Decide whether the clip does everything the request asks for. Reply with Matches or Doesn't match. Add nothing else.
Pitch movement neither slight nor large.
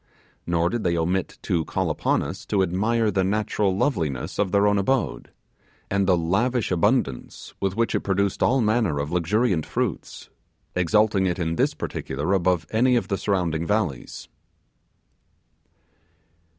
Matches